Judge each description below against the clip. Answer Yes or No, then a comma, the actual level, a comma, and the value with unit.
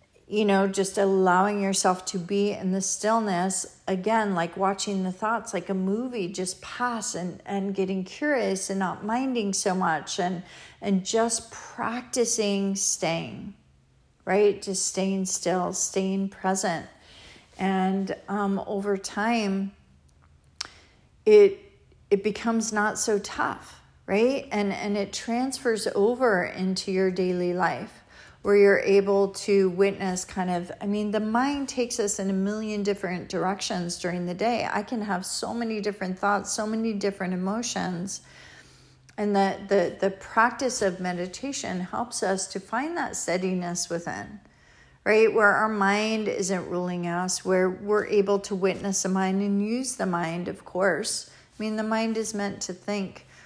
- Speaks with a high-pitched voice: Yes, high, 200 Hz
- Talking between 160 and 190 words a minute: No, average, 150 wpm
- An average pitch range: No, narrow, 2.3 semitones